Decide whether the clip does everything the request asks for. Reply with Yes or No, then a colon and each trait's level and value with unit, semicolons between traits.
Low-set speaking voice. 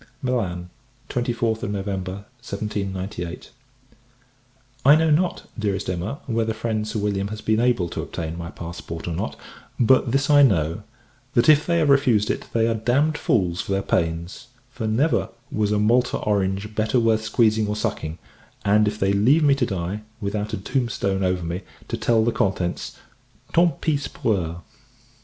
Yes: low, 105 Hz